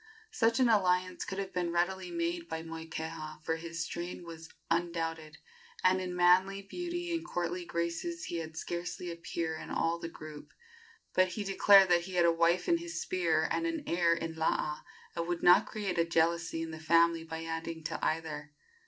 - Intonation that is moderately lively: No, narrow, 2.2 semitones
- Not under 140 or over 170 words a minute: No, average, 190 wpm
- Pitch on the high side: No, medium, 170 Hz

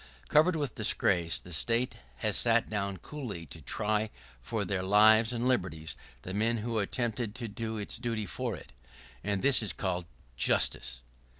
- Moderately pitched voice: No, low, 105 Hz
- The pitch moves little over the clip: No, average, 4.0 semitones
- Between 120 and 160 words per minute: No, average, 170 wpm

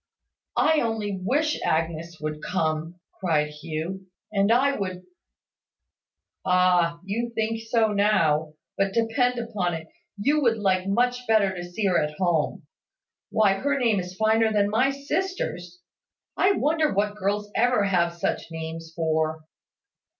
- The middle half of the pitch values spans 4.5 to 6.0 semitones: Yes, average, 5.1 semitones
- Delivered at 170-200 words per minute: No, average, 145 wpm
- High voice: Yes, high, 195 Hz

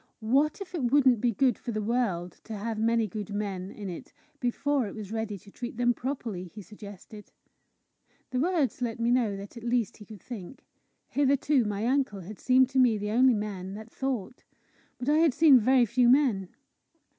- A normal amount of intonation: Yes, average, 3.7 semitones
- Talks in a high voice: Yes, high, 230 Hz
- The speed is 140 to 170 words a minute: No, average, 195 wpm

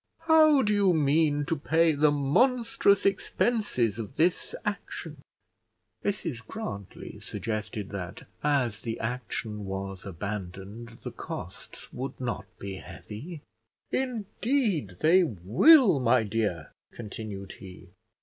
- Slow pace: Yes, slow, 110 wpm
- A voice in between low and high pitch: No, low, 125 Hz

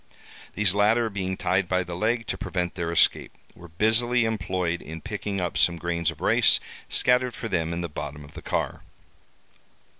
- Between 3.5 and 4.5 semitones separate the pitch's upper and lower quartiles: Yes, average, 4.2 semitones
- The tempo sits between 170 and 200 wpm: Yes, average, 180 wpm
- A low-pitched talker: Yes, very low, 90 Hz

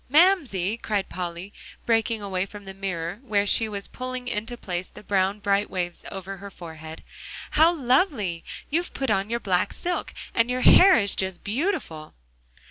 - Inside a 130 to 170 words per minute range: Yes, average, 165 wpm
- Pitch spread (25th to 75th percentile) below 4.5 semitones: No, average, 4.9 semitones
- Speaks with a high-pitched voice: Yes, high, 205 Hz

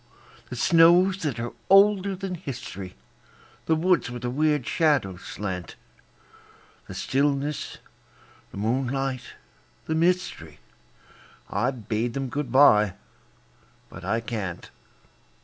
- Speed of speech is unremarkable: No, slow, 110 wpm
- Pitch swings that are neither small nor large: No, wide, 6.0 semitones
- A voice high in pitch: No, low, 135 Hz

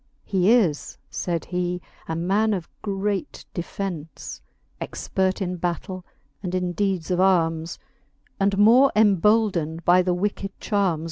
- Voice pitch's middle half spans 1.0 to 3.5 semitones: Yes, narrow, 2.4 semitones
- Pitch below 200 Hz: Yes, medium, 185 Hz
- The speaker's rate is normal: No, slow, 130 wpm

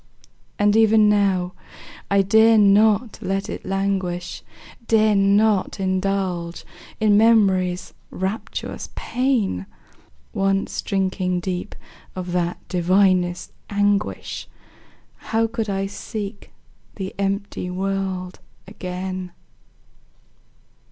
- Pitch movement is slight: Yes, narrow, 2.1 semitones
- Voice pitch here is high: Yes, high, 195 Hz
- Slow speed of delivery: Yes, slow, 90 wpm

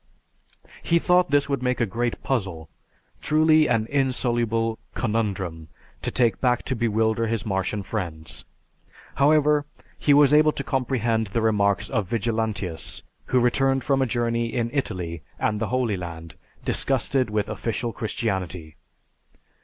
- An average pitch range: Yes, average, 4.5 semitones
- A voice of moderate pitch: No, low, 115 Hz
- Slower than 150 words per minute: Yes, average, 140 wpm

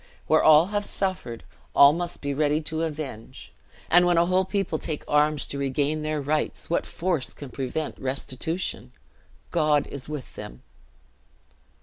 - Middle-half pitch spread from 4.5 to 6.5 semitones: No, average, 3.2 semitones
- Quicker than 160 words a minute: No, average, 155 wpm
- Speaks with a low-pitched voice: No, medium, 155 Hz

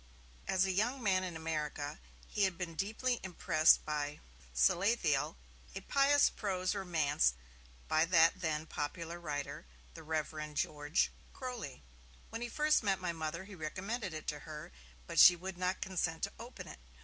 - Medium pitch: Yes, medium, 170 Hz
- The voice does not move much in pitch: No, average, 4.1 semitones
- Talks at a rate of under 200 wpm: Yes, average, 160 wpm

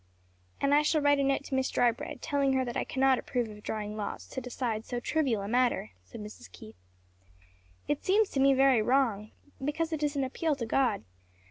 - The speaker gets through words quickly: Yes, fast, 210 wpm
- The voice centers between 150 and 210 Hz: No, very high, 265 Hz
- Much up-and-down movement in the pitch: No, average, 3.8 semitones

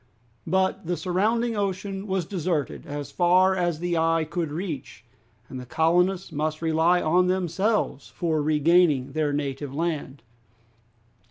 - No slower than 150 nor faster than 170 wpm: No, slow, 135 wpm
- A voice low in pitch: No, medium, 170 Hz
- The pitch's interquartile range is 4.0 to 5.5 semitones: No, average, 3.4 semitones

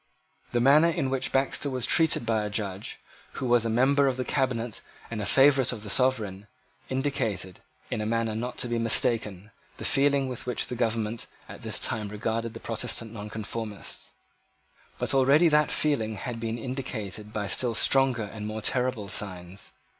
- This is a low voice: Yes, low, 115 Hz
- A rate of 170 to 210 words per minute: Yes, average, 175 wpm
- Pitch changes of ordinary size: Yes, average, 3.5 semitones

